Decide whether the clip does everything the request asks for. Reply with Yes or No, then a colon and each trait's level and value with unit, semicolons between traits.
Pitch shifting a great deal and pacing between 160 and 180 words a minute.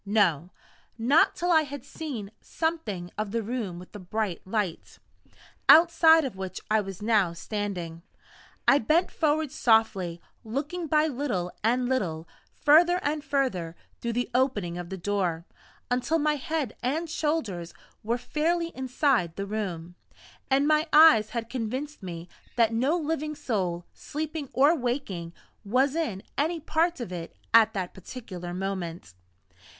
No: wide, 8.0 semitones; average, 145 wpm